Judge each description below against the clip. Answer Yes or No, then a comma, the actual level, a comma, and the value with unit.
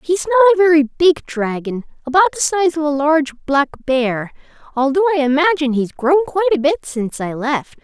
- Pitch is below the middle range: No, very high, 300 Hz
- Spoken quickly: No, average, 190 wpm